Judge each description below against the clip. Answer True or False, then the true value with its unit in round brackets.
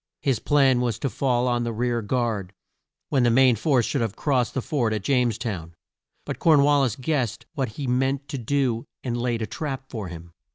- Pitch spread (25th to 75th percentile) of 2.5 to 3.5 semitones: True (3.0 semitones)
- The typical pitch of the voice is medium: False (125 Hz)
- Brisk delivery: True (210 wpm)